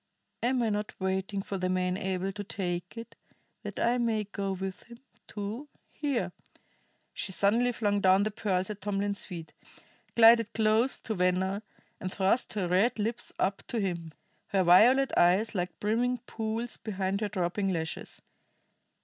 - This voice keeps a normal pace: Yes, average, 160 wpm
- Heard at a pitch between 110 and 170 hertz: No, high, 200 Hz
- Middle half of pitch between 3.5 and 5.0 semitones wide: No, average, 3.1 semitones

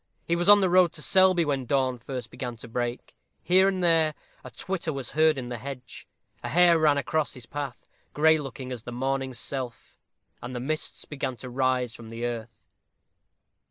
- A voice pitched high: No, low, 135 Hz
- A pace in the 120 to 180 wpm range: No, average, 195 wpm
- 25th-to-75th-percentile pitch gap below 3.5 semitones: No, average, 4.4 semitones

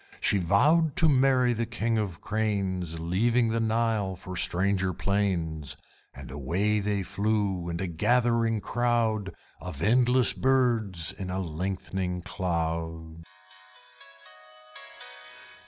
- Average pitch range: Yes, average, 4.5 semitones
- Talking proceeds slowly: Yes, slow, 115 wpm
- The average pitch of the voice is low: Yes, low, 100 Hz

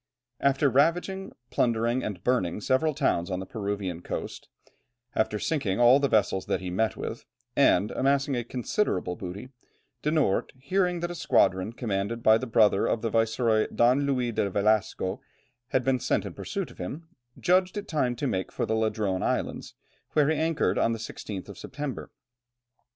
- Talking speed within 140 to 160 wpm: No, average, 175 wpm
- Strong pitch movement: Yes, wide, 5.7 semitones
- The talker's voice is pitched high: No, low, 115 Hz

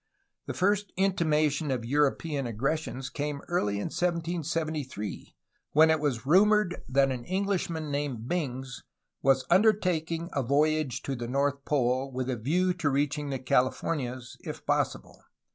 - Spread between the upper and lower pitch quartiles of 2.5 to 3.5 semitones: No, average, 4.3 semitones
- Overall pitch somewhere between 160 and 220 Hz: No, medium, 145 Hz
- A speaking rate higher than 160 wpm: No, average, 140 wpm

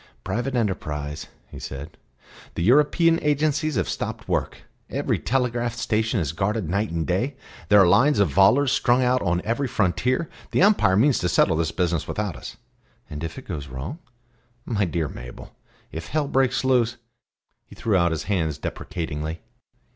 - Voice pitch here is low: Yes, low, 105 Hz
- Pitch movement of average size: No, wide, 7.3 semitones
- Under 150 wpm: No, average, 170 wpm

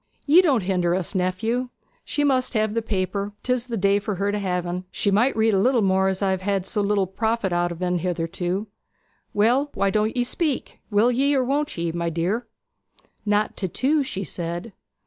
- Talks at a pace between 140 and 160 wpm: No, fast, 205 wpm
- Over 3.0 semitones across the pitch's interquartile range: Yes, average, 4.4 semitones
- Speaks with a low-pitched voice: No, high, 205 Hz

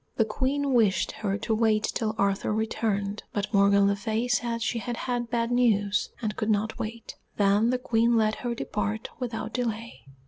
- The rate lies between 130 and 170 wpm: No, average, 180 wpm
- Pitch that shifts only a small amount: Yes, narrow, 2.2 semitones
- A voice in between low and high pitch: No, high, 220 Hz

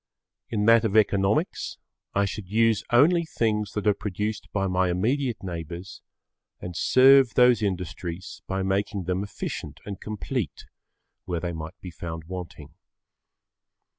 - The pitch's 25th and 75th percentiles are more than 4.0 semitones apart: No, average, 3.4 semitones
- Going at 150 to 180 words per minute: No, average, 140 wpm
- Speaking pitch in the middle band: No, low, 100 Hz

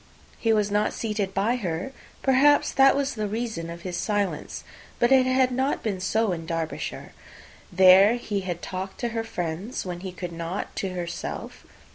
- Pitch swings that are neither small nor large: Yes, average, 4.9 semitones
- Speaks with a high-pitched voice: Yes, high, 200 Hz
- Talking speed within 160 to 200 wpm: Yes, average, 175 wpm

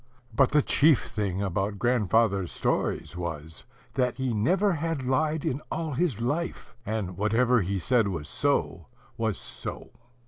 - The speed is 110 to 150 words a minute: Yes, average, 145 wpm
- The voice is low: Yes, low, 115 Hz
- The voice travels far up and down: Yes, wide, 6.3 semitones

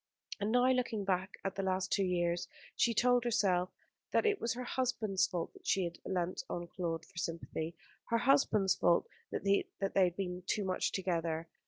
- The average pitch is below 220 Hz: Yes, high, 190 Hz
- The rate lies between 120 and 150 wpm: No, average, 185 wpm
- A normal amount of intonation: Yes, average, 4.2 semitones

